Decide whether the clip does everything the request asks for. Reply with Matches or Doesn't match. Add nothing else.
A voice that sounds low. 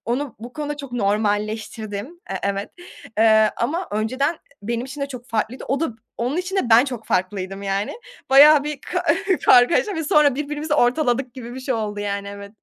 Doesn't match